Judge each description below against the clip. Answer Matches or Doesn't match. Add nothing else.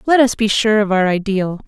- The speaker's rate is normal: Doesn't match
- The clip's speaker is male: Doesn't match